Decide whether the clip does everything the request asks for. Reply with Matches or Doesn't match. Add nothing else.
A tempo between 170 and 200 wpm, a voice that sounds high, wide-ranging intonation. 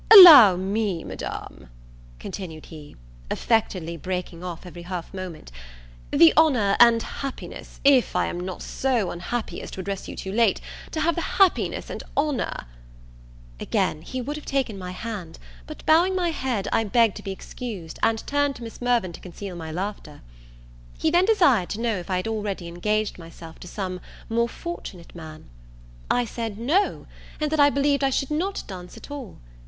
Matches